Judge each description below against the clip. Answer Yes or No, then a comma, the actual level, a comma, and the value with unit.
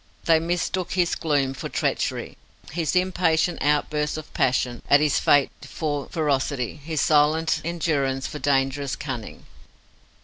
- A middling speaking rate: No, slow, 130 wpm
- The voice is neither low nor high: Yes, medium, 150 Hz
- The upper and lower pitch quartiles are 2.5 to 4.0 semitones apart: Yes, average, 2.8 semitones